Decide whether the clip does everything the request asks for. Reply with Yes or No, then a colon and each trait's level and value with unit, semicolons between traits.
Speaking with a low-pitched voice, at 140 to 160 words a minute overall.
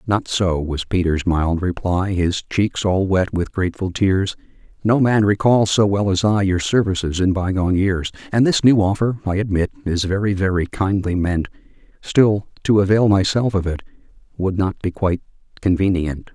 No: very low, 95 Hz; average, 175 wpm